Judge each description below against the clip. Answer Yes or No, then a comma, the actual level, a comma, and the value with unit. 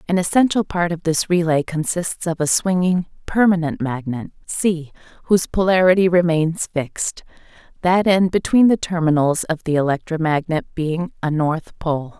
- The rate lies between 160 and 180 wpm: No, average, 145 wpm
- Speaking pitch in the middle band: Yes, medium, 170 Hz